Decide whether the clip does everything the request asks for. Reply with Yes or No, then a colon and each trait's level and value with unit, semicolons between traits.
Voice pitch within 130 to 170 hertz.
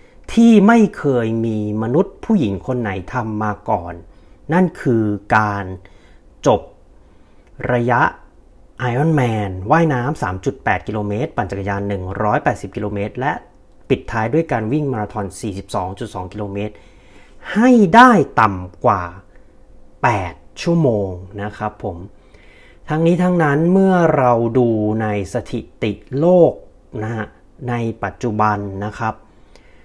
No: low, 110 Hz